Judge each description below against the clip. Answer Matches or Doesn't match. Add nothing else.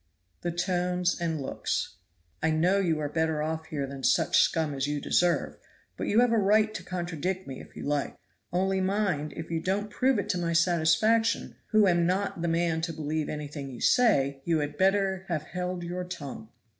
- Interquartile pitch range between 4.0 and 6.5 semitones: Doesn't match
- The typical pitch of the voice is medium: Matches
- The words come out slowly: Doesn't match